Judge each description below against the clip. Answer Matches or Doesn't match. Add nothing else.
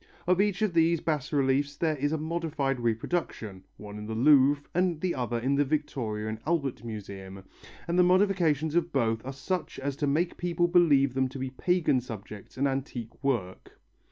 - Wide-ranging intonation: Matches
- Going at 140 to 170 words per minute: Doesn't match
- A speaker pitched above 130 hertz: Matches